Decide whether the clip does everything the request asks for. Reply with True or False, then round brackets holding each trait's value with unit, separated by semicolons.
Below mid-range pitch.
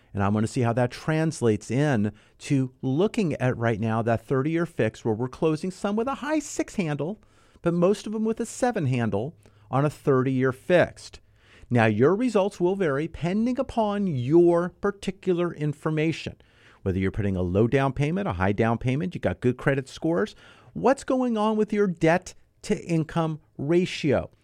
False (150 Hz)